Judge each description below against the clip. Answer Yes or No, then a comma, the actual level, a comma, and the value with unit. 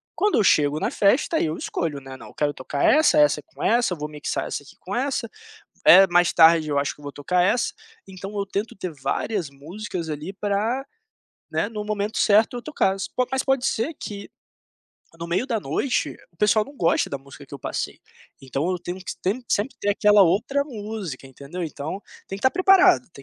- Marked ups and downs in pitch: Yes, wide, 6.4 semitones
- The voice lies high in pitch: Yes, high, 195 Hz